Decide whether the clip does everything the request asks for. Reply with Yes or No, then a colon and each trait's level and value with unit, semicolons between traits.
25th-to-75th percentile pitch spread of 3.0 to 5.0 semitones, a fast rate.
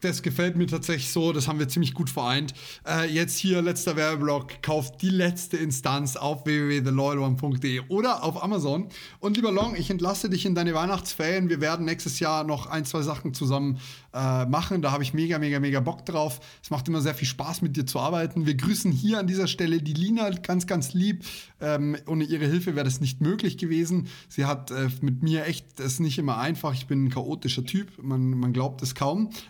Yes: average, 3.8 semitones; fast, 210 wpm